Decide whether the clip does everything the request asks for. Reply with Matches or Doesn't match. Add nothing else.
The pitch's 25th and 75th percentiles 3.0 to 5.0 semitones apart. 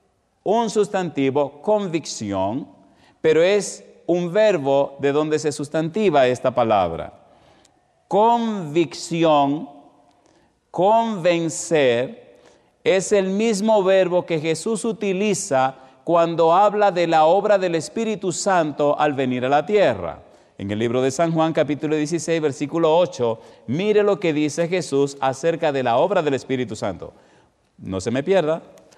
Doesn't match